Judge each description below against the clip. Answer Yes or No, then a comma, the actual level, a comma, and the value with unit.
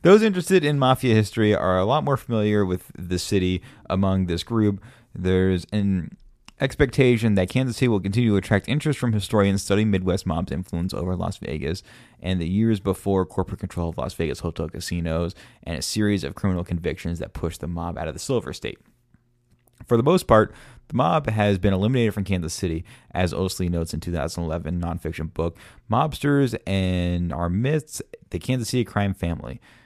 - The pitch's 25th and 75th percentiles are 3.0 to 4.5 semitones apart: No, average, 4.9 semitones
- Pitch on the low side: Yes, very low, 95 Hz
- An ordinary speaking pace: Yes, average, 180 wpm